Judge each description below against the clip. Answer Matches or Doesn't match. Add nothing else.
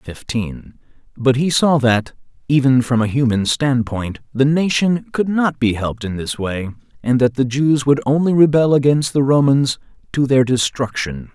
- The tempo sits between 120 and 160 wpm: Doesn't match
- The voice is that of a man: Matches